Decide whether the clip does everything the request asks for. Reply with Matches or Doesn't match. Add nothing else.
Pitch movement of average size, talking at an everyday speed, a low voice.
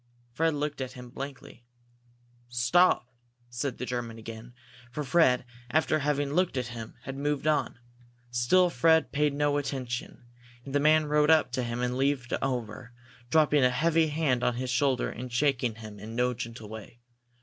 Matches